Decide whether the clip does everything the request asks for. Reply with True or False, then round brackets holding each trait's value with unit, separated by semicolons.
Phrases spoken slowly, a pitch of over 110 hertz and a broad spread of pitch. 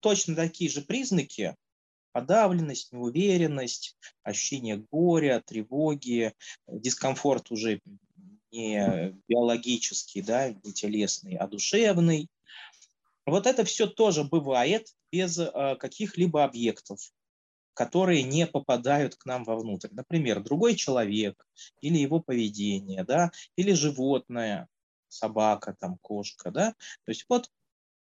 True (105 wpm; 140 Hz; 7.6 semitones)